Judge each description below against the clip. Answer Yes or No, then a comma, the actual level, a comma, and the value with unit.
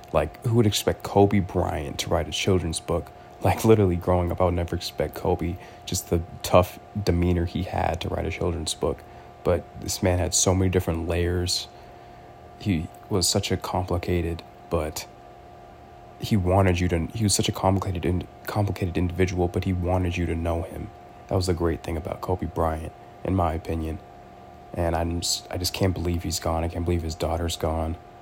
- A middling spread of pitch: No, narrow, 2.2 semitones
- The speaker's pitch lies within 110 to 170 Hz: No, very low, 90 Hz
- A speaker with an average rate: Yes, average, 190 wpm